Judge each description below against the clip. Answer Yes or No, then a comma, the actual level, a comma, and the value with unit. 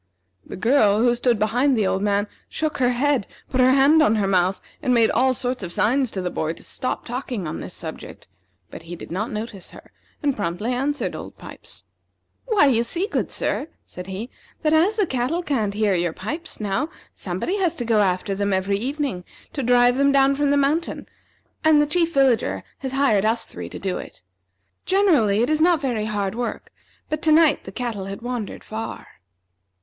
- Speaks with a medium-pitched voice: No, high, 245 Hz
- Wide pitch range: Yes, wide, 5.8 semitones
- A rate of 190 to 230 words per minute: Yes, average, 200 wpm